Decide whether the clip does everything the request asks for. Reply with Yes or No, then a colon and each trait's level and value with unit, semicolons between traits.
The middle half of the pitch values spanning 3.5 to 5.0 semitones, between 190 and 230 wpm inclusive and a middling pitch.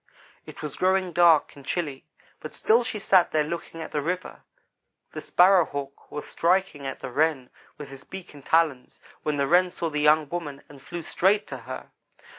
Yes: average, 3.9 semitones; average, 195 wpm; medium, 155 Hz